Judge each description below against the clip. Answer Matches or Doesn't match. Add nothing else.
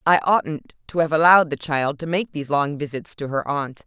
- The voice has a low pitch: Doesn't match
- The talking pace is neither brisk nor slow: Doesn't match